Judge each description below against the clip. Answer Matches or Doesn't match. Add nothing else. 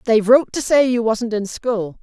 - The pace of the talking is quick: Matches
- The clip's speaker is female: Matches